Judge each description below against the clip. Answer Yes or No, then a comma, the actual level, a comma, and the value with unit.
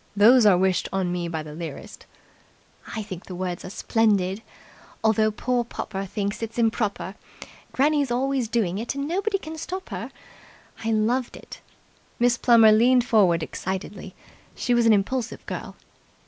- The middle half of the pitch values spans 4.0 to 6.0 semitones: Yes, average, 4.3 semitones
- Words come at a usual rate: Yes, average, 155 wpm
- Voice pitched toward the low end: No, high, 220 Hz